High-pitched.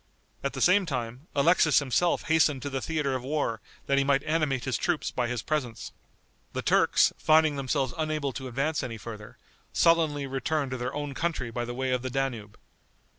No: low, 135 Hz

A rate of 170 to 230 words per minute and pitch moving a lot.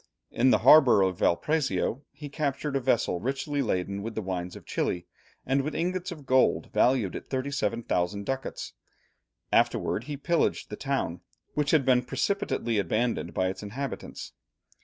No: average, 155 wpm; wide, 5.9 semitones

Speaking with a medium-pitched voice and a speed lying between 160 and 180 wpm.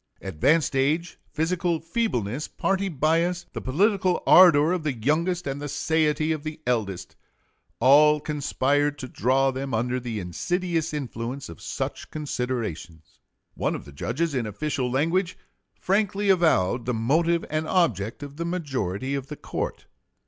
No: medium, 145 Hz; average, 145 wpm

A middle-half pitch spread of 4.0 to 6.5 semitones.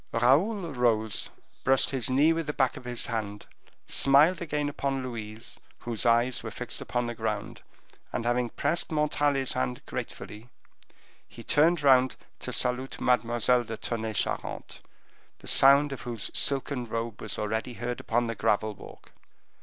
No: average, 3.3 semitones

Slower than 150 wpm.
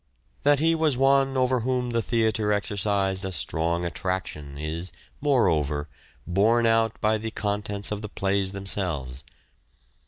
Yes: slow, 135 wpm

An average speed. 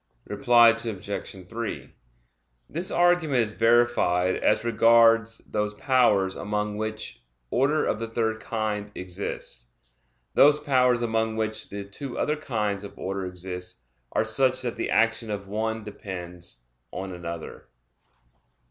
No: slow, 130 wpm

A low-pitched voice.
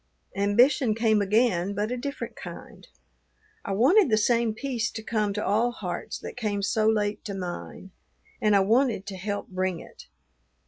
No: high, 215 Hz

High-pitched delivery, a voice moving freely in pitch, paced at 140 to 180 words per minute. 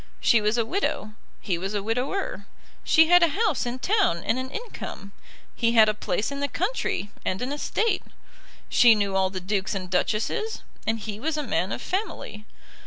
No: high, 230 Hz; wide, 7.9 semitones; average, 190 wpm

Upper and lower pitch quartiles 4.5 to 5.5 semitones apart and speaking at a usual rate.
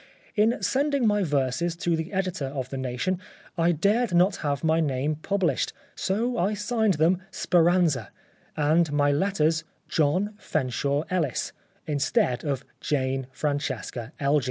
Yes: average, 5.0 semitones; average, 145 wpm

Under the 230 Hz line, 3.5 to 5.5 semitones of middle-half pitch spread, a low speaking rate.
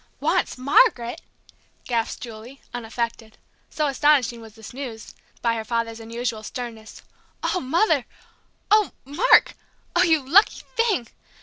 No: high, 245 Hz; average, 4.9 semitones; slow, 120 wpm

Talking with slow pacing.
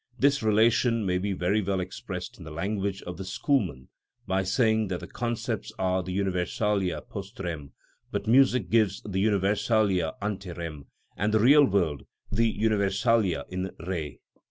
No: average, 155 wpm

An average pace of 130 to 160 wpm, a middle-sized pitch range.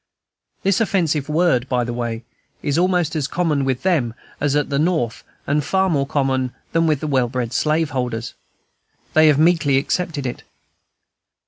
Yes: average, 155 wpm; average, 4.2 semitones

